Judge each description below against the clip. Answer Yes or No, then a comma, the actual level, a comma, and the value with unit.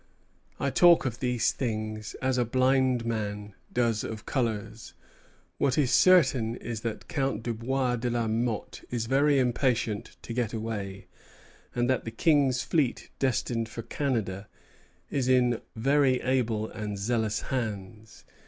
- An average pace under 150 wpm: Yes, average, 140 wpm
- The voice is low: Yes, low, 120 Hz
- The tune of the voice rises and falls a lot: No, average, 2.9 semitones